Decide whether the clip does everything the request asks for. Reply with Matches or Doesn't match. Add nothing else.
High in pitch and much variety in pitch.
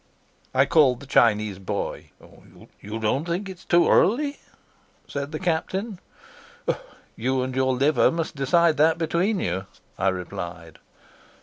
Doesn't match